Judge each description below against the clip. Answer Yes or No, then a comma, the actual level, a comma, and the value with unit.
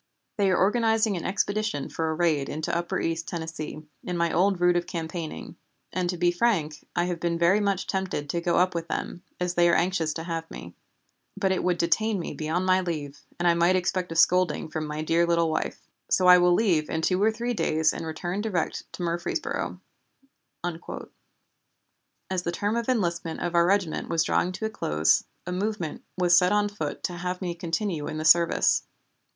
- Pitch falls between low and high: Yes, medium, 175 Hz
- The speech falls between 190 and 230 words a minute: Yes, average, 200 wpm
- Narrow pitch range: Yes, narrow, 2.2 semitones